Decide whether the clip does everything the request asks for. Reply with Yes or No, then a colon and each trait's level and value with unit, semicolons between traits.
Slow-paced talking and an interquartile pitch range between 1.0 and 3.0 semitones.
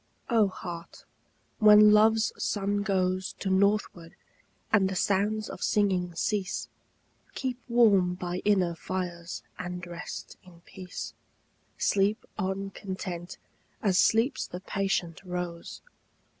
Yes: slow, 115 wpm; narrow, 2.6 semitones